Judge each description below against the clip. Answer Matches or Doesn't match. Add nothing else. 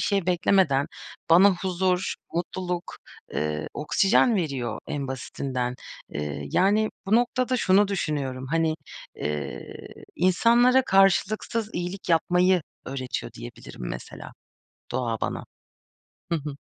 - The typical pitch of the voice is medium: Matches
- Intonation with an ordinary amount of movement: Doesn't match